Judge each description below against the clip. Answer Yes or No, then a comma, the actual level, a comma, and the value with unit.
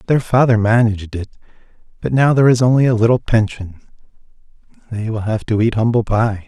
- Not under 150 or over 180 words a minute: Yes, average, 175 wpm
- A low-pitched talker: Yes, low, 110 Hz